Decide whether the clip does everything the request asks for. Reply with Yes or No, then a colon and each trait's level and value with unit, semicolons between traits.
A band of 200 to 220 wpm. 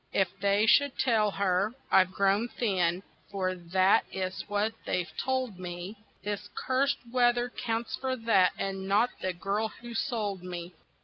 No: average, 150 wpm